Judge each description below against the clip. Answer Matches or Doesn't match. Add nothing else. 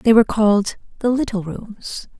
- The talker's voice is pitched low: Doesn't match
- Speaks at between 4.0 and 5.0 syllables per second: Matches